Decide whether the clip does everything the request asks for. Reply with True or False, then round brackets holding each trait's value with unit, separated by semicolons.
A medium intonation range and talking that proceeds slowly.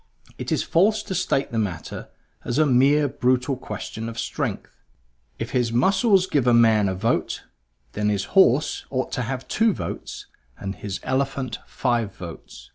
False (4.3 semitones; 165 wpm)